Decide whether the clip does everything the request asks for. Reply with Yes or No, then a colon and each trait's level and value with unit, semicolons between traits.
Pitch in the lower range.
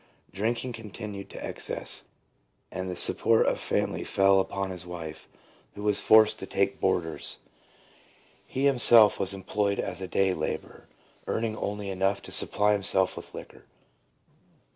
Yes: low, 100 Hz